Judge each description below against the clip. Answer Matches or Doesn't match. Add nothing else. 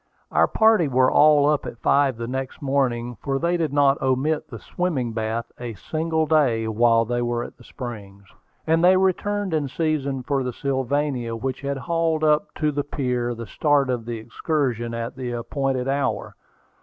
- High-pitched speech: Doesn't match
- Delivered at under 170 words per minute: Doesn't match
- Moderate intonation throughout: Matches